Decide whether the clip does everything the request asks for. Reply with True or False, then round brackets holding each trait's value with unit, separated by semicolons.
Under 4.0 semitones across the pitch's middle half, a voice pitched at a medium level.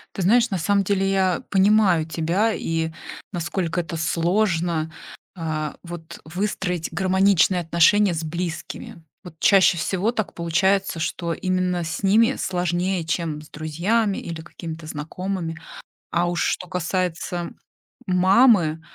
True (2.8 semitones; 175 Hz)